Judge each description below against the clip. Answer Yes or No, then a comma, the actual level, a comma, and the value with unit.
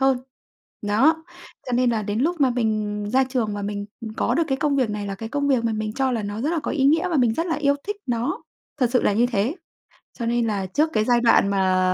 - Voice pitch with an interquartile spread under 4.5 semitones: No, average, 4.8 semitones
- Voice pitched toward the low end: No, high, 240 Hz